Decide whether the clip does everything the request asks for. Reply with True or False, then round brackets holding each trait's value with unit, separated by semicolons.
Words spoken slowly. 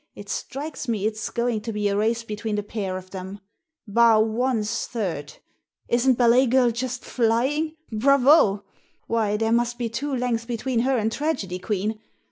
False (165 wpm)